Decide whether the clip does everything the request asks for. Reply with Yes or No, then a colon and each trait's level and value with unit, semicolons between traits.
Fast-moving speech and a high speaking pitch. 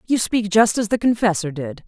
Yes: fast, 225 wpm; high, 205 Hz